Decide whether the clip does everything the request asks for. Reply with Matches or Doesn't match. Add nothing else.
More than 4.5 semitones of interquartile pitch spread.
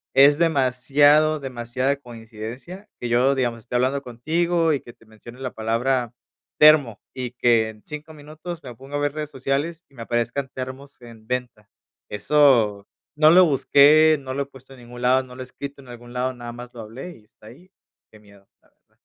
Doesn't match